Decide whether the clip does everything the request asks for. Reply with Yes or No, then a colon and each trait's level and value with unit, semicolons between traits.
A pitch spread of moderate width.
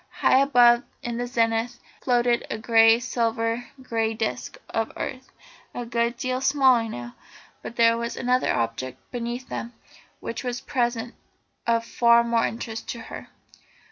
No: narrow, 1.2 semitones